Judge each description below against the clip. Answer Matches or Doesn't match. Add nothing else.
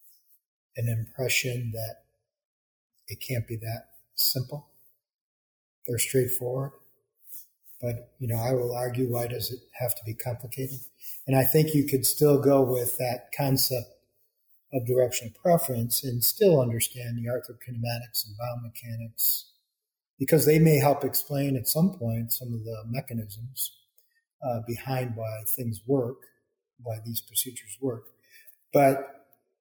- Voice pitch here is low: Matches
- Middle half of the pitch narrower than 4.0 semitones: Matches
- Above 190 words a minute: Doesn't match